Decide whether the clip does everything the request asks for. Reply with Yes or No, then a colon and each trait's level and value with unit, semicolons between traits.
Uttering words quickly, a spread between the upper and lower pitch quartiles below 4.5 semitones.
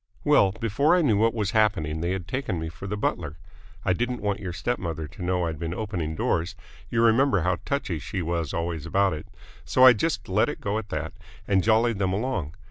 No: fast, 220 wpm; average, 4.9 semitones